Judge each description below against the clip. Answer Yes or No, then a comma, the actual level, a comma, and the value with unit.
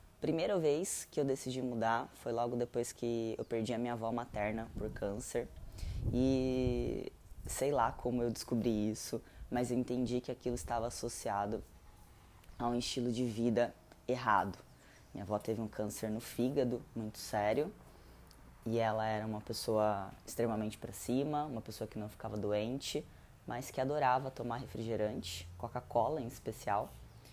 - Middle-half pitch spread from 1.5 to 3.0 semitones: Yes, narrow, 2.4 semitones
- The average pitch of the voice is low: Yes, low, 115 Hz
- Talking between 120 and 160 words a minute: Yes, average, 150 wpm